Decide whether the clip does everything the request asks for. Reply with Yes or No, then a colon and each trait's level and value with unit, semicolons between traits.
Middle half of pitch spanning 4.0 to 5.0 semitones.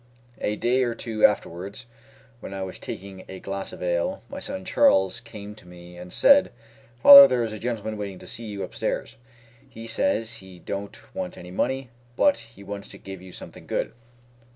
No: average, 3.4 semitones